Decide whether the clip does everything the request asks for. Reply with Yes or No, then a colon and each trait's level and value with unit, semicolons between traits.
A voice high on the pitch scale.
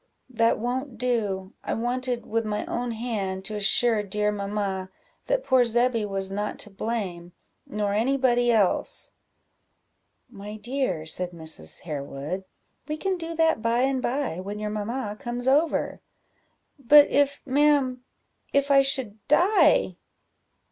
Yes: high, 230 Hz